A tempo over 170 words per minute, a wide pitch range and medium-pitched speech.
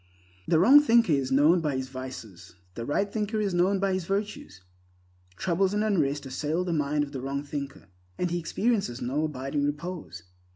Yes: average, 180 wpm; wide, 6.1 semitones; medium, 150 Hz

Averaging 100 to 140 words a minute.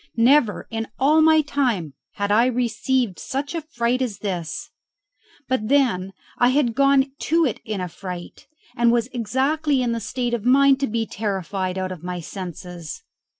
No: average, 170 wpm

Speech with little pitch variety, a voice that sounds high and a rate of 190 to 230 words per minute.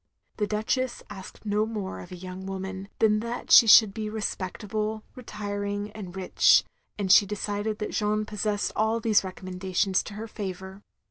No: narrow, 2.0 semitones; high, 205 Hz; average, 160 wpm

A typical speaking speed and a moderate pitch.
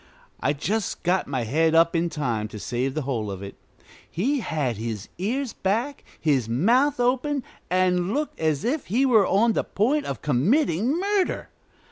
Yes: average, 170 wpm; medium, 180 Hz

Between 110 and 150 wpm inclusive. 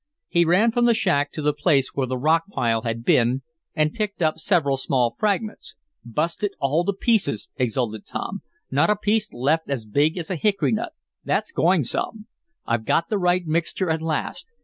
No: average, 195 wpm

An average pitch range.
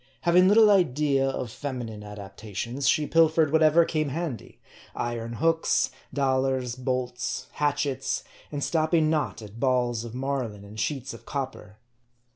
Yes: average, 4.4 semitones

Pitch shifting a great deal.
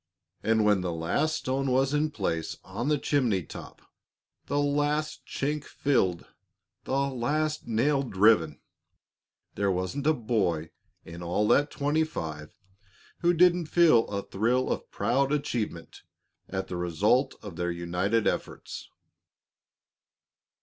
Yes: wide, 7.8 semitones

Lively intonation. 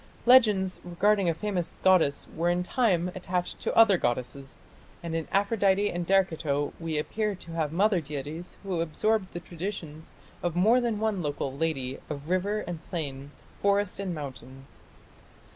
No: average, 4.3 semitones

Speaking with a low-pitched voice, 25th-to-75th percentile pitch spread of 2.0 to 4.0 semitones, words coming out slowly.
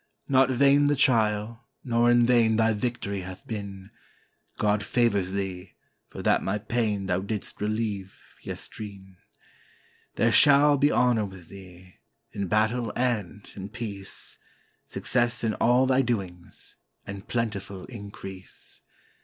Yes: low, 110 Hz; average, 3.5 semitones; slow, 130 wpm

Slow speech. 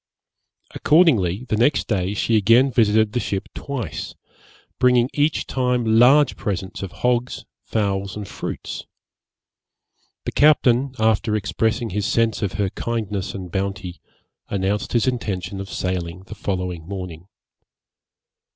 Yes: slow, 125 wpm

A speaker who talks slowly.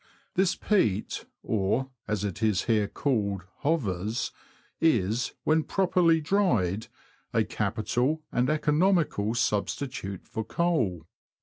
Yes: slow, 110 wpm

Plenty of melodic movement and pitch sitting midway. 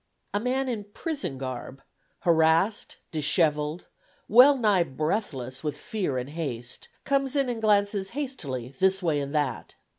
Yes: wide, 7.6 semitones; medium, 175 Hz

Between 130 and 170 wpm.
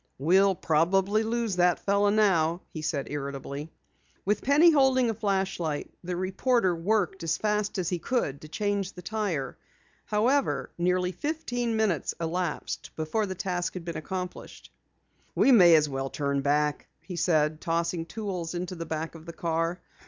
Yes: average, 160 wpm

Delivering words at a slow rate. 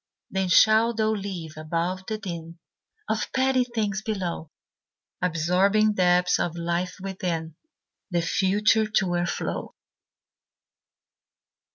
Yes: slow, 100 wpm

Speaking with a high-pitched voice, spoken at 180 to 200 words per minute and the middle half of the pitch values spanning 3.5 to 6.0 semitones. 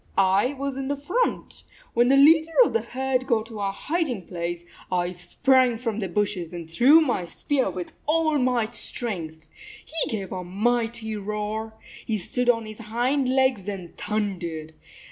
No: high, 225 Hz; average, 165 wpm; wide, 5.4 semitones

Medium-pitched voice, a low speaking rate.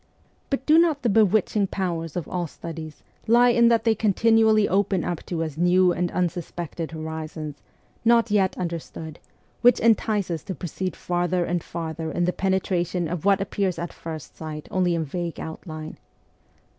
No: medium, 180 Hz; average, 170 wpm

